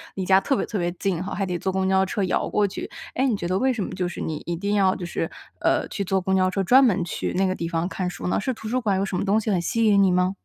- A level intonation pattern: Yes, narrow, 2.1 semitones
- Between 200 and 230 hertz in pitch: No, high, 190 Hz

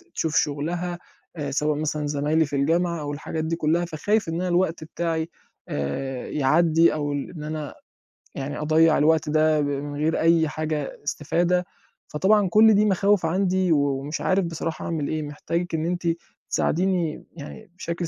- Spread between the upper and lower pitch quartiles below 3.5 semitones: Yes, average, 2.7 semitones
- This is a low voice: No, medium, 160 Hz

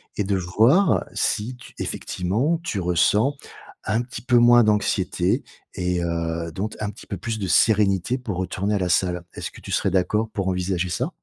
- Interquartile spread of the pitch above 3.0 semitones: Yes, average, 3.8 semitones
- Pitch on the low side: Yes, low, 100 Hz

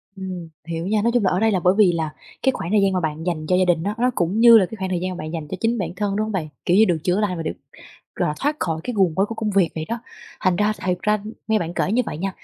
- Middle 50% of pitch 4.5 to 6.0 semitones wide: No, average, 3.8 semitones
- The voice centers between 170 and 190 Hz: Yes, medium, 185 Hz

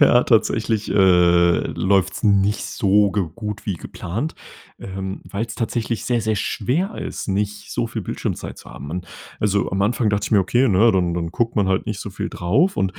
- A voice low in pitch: Yes, low, 105 Hz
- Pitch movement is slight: No, average, 3.1 semitones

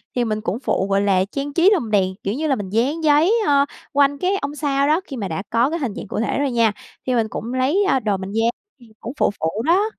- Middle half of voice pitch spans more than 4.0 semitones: Yes, average, 5.3 semitones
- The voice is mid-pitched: No, very high, 250 Hz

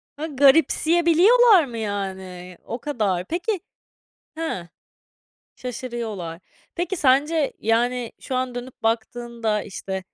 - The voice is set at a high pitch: Yes, high, 245 Hz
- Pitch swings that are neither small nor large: No, wide, 6.8 semitones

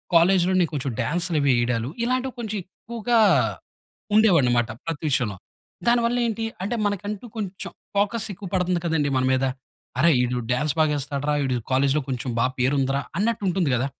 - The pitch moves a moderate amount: No, wide, 7.6 semitones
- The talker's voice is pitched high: No, medium, 165 Hz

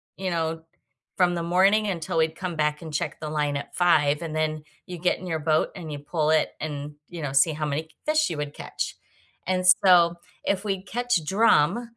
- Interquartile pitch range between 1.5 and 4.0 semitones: Yes, average, 3.2 semitones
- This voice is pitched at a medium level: Yes, medium, 165 Hz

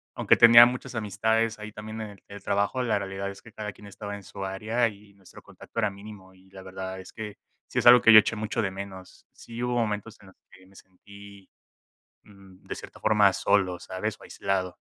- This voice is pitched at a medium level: No, low, 100 Hz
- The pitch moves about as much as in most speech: No, narrow, 2.3 semitones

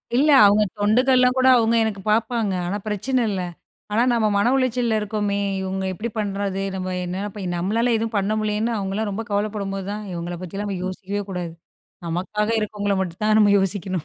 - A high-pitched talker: Yes, high, 205 Hz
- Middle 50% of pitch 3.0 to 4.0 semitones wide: No, narrow, 2.4 semitones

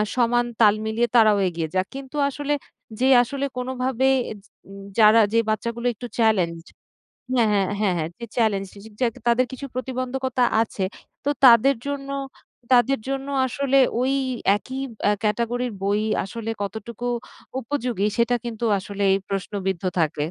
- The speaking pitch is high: Yes, high, 235 Hz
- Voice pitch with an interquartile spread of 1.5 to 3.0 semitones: No, average, 3.7 semitones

